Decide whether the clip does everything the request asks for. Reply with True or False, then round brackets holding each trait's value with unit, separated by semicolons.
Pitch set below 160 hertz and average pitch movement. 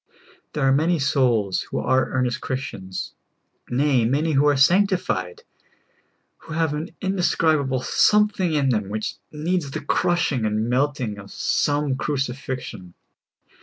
True (140 Hz; 4.4 semitones)